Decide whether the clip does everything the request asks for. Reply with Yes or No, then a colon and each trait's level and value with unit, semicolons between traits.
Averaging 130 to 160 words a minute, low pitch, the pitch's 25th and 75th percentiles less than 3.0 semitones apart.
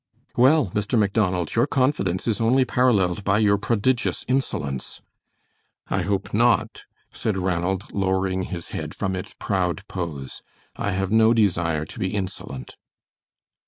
No: slow, 135 wpm; low, 100 Hz; average, 3.8 semitones